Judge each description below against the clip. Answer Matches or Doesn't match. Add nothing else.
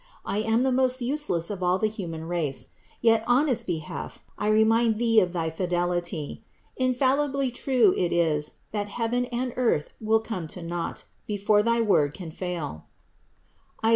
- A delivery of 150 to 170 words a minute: Matches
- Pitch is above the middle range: Matches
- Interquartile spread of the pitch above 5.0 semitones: Matches